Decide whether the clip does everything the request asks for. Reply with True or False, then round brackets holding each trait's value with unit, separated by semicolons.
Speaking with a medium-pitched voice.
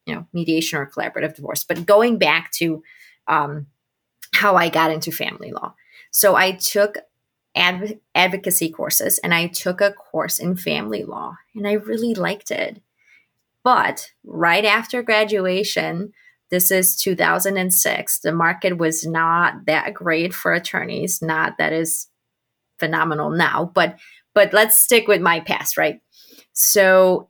True (180 Hz)